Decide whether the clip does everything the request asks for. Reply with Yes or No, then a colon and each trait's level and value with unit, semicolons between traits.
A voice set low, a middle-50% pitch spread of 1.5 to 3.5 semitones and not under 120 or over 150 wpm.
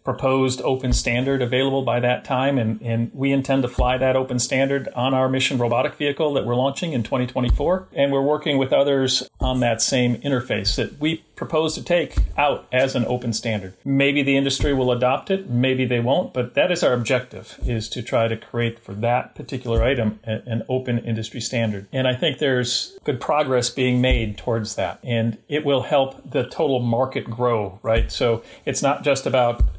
No: low, 130 Hz; narrow, 2.5 semitones; average, 195 wpm